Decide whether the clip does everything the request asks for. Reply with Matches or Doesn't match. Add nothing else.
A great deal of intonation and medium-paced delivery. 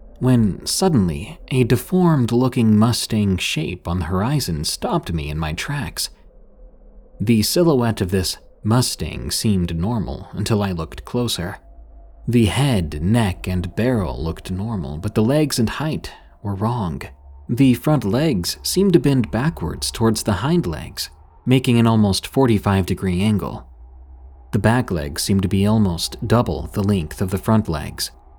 Matches